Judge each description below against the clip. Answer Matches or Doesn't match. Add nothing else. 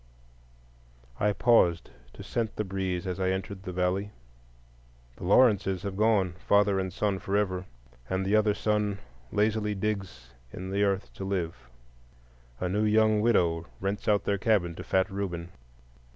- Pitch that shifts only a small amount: Matches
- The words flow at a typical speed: Matches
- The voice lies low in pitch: Matches